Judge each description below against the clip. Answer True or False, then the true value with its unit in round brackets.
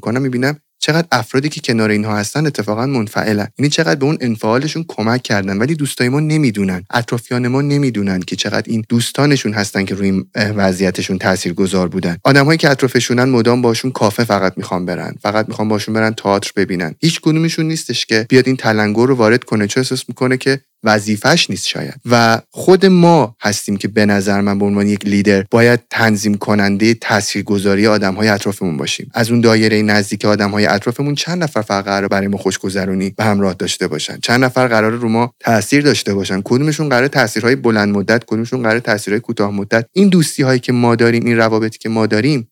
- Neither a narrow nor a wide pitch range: True (4.1 semitones)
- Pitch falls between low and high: False (110 Hz)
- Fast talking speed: True (190 wpm)